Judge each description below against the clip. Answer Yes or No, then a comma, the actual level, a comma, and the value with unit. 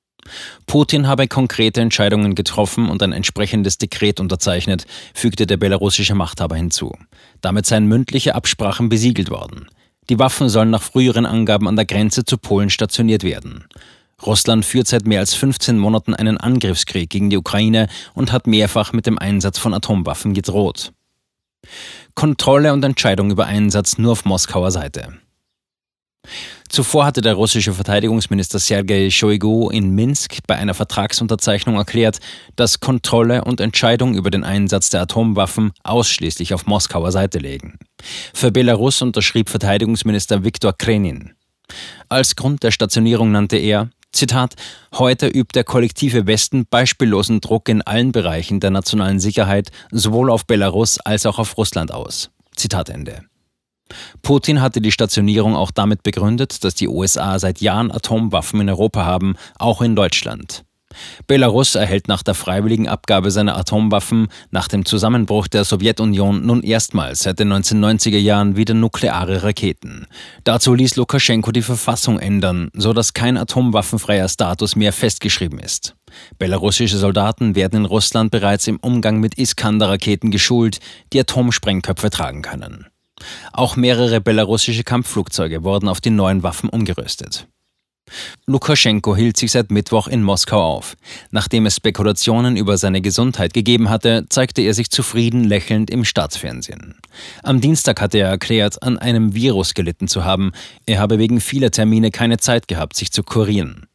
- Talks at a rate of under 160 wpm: Yes, average, 145 wpm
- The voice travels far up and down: No, average, 2.8 semitones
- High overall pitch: No, low, 110 Hz